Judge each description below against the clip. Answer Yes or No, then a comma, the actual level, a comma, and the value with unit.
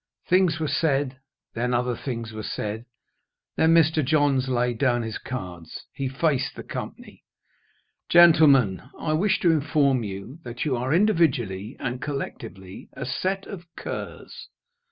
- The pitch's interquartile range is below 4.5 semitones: No, average, 4.8 semitones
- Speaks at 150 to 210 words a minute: No, average, 140 wpm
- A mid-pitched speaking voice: No, low, 130 Hz